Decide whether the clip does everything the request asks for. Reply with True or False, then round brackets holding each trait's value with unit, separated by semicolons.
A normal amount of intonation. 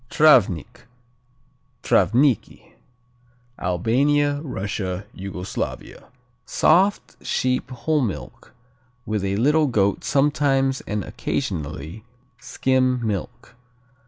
False (6.4 semitones)